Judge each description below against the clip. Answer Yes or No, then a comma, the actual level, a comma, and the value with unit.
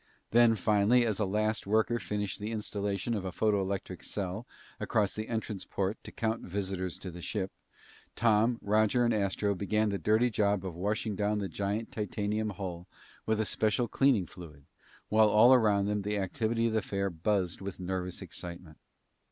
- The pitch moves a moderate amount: No, narrow, 2.3 semitones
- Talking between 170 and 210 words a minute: Yes, average, 175 wpm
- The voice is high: No, low, 105 Hz